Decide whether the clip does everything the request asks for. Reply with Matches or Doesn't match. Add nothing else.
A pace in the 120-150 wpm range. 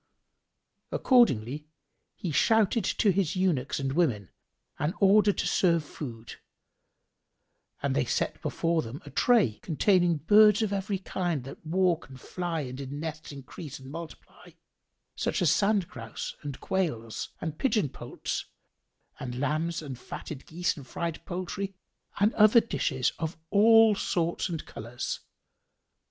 Matches